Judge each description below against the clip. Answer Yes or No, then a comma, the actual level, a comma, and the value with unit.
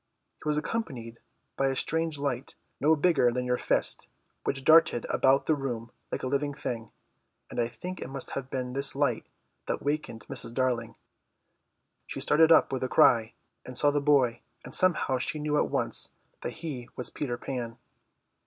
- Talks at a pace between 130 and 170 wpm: No, average, 180 wpm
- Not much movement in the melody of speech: No, average, 3.3 semitones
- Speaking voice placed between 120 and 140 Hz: Yes, low, 135 Hz